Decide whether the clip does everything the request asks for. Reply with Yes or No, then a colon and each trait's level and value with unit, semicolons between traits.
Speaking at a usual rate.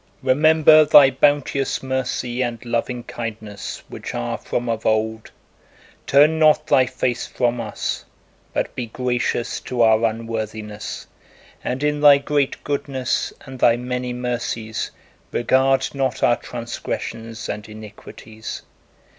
No: slow, 120 wpm